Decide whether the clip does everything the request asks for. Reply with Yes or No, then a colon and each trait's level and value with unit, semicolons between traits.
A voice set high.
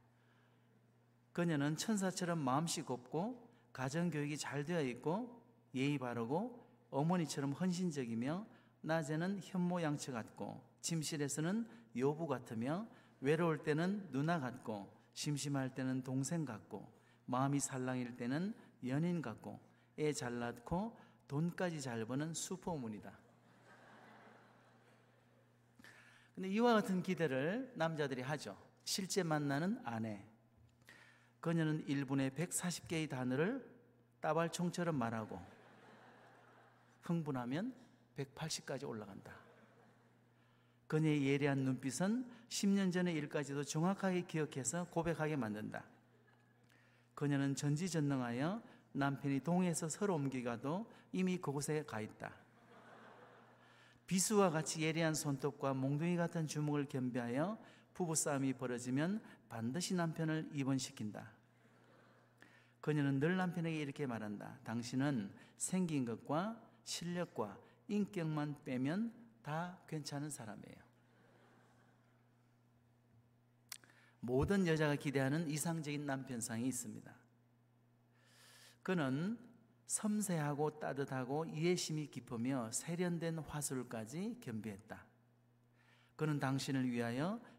No: medium, 145 Hz